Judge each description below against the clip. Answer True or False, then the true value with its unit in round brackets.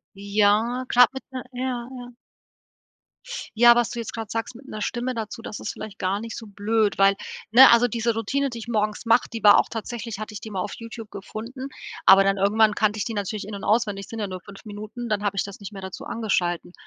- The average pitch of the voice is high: True (220 Hz)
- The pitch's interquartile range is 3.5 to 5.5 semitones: False (2.6 semitones)